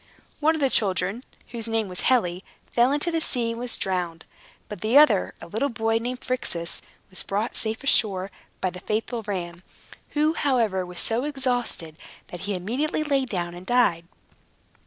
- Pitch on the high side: Yes, high, 225 Hz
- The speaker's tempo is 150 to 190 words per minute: Yes, average, 175 wpm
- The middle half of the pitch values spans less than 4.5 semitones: No, wide, 5.6 semitones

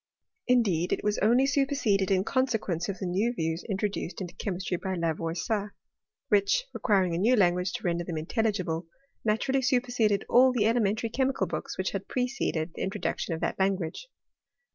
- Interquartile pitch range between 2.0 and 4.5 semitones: No, average, 5.3 semitones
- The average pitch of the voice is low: No, high, 200 Hz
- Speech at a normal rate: Yes, average, 165 wpm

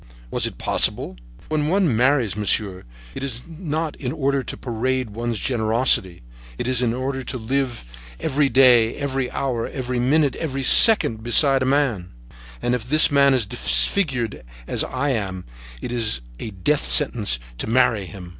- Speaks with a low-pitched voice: Yes, low, 125 Hz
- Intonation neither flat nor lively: Yes, average, 3.8 semitones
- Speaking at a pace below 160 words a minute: No, average, 165 wpm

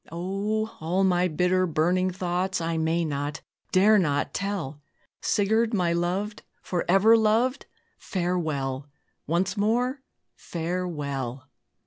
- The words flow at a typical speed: No, slow, 105 wpm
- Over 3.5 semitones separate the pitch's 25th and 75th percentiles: Yes, average, 3.9 semitones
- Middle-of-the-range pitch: Yes, medium, 180 Hz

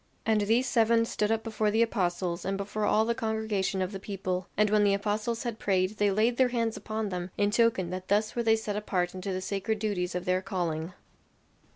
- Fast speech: Yes, fast, 220 wpm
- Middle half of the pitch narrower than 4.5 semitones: Yes, average, 2.9 semitones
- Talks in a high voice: Yes, high, 205 Hz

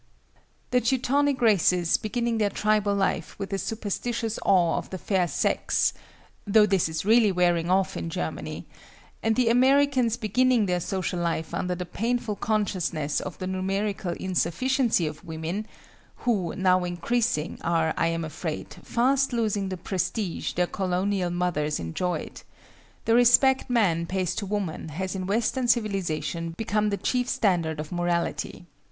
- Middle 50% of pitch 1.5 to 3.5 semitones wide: No, average, 4.6 semitones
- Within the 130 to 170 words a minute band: Yes, average, 145 wpm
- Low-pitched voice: No, high, 195 Hz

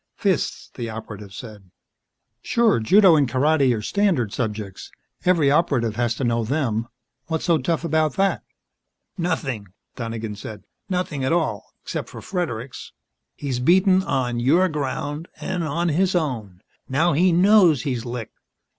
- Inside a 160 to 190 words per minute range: No, average, 145 wpm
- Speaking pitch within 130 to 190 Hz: Yes, medium, 140 Hz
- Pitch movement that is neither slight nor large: No, wide, 6.7 semitones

